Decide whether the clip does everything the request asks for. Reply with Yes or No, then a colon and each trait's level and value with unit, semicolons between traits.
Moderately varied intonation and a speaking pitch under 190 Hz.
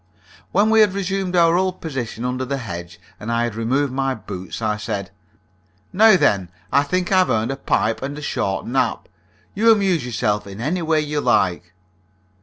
No: wide, 8.5 semitones; low, 135 Hz